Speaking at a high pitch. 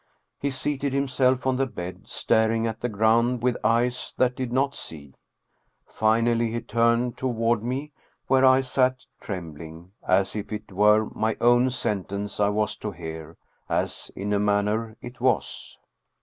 No: low, 115 Hz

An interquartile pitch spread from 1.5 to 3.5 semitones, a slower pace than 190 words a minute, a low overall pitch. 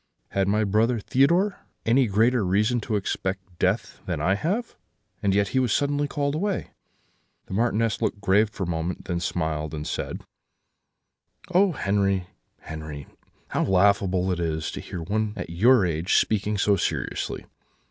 No: average, 4.5 semitones; average, 155 wpm; low, 100 Hz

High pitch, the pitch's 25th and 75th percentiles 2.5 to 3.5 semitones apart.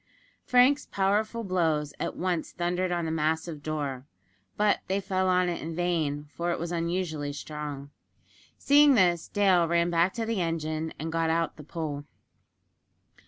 No: medium, 170 Hz; average, 3.0 semitones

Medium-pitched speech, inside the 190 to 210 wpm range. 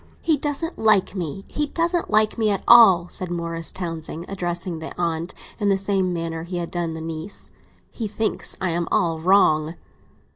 No: medium, 180 Hz; average, 175 wpm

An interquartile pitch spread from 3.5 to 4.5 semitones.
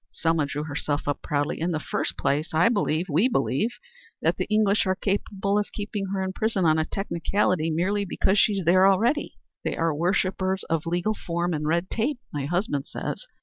Yes: average, 4.2 semitones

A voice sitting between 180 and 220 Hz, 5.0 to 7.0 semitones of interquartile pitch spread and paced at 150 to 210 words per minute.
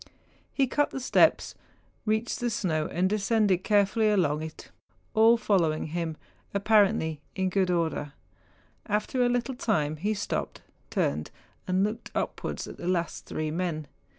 No: high, 190 Hz; average, 5.3 semitones; average, 140 wpm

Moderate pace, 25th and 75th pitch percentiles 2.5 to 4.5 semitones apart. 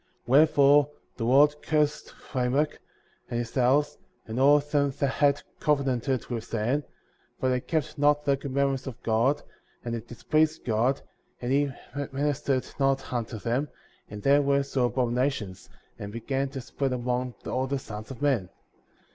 Yes: average, 160 wpm; average, 2.8 semitones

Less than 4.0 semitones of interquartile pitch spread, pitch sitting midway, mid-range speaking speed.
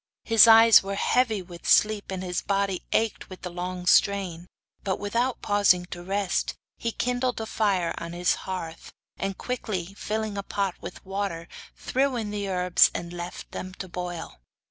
No: average, 3.2 semitones; high, 195 Hz; average, 170 wpm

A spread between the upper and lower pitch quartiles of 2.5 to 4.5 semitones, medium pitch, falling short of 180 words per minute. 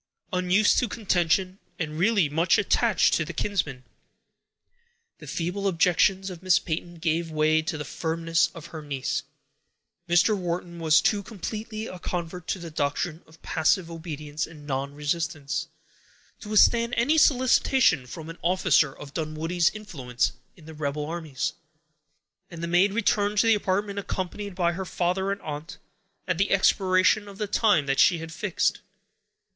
Yes: average, 3.9 semitones; medium, 175 Hz; average, 155 wpm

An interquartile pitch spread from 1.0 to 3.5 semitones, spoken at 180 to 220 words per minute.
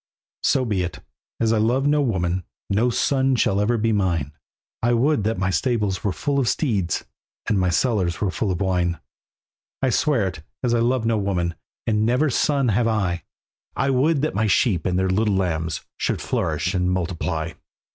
No: average, 5.1 semitones; average, 190 wpm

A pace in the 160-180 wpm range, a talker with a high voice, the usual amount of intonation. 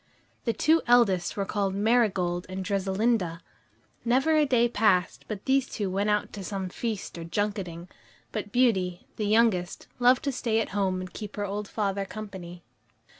Yes: average, 170 wpm; high, 205 Hz; average, 3.7 semitones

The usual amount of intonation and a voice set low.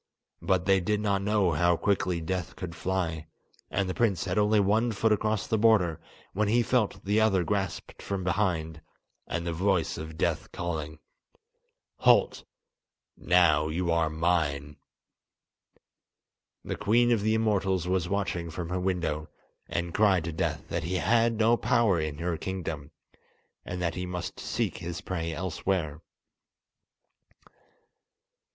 Yes: average, 3.6 semitones; very low, 90 Hz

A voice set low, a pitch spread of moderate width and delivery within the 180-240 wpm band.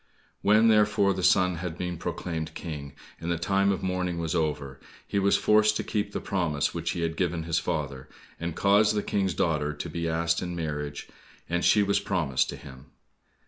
Yes: very low, 85 Hz; average, 3.7 semitones; average, 195 wpm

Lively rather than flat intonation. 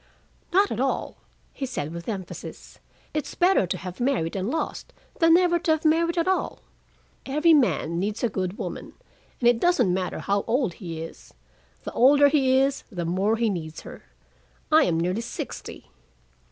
Yes: wide, 8.8 semitones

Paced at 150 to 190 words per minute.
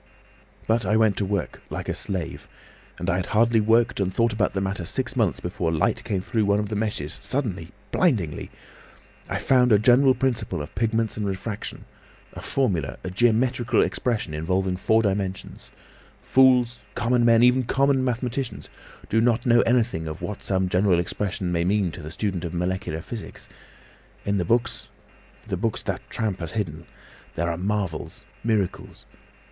Yes: average, 160 wpm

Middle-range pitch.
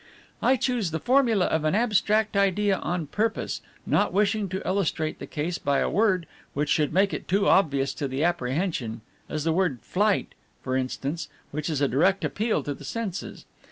Yes: medium, 180 Hz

